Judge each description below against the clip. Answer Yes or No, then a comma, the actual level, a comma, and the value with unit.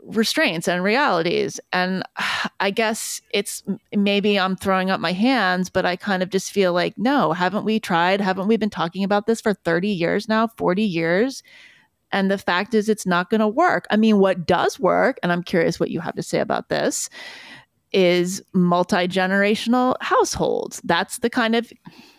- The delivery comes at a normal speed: Yes, average, 185 wpm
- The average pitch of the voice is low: No, high, 200 Hz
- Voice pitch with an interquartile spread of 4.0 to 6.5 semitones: No, average, 3.6 semitones